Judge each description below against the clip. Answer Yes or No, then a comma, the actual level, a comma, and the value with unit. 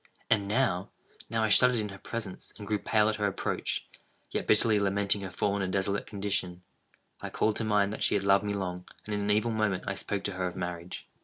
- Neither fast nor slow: No, fast, 225 wpm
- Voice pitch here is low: Yes, low, 100 Hz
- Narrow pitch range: Yes, narrow, 1.7 semitones